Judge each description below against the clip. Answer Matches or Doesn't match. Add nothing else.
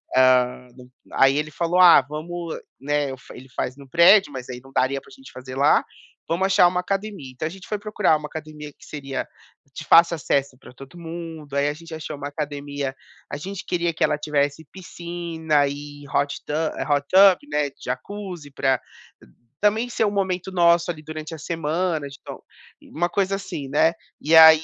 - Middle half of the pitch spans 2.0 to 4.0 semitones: Matches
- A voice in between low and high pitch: Matches